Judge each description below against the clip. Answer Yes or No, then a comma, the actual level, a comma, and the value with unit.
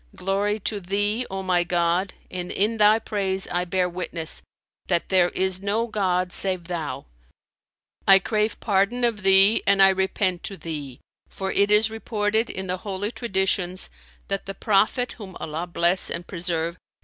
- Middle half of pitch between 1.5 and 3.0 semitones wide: Yes, narrow, 2.5 semitones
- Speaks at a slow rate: No, average, 160 wpm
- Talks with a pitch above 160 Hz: Yes, high, 190 Hz